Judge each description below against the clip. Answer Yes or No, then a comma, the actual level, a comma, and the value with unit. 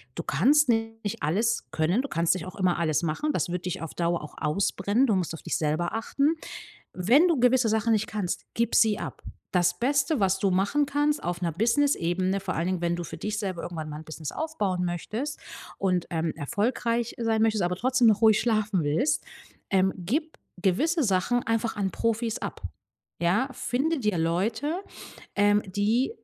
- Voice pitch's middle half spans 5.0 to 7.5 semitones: Yes, average, 5.3 semitones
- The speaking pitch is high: Yes, high, 205 Hz